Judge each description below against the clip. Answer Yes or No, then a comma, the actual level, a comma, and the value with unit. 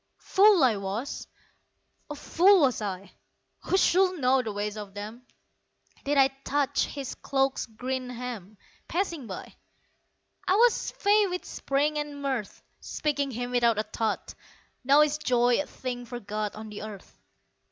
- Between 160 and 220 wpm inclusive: No, average, 150 wpm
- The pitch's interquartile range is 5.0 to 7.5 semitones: Yes, average, 5.3 semitones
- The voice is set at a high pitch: Yes, very high, 255 Hz